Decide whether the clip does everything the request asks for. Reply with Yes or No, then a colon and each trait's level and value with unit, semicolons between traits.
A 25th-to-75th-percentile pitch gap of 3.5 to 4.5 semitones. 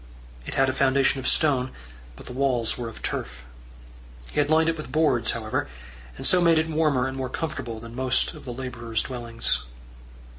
Yes: average, 4.1 semitones